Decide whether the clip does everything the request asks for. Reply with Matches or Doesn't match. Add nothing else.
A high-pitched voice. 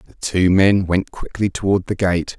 Doesn't match